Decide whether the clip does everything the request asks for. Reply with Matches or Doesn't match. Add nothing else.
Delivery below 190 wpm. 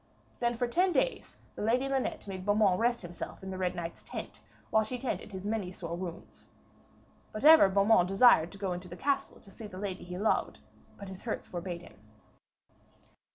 Doesn't match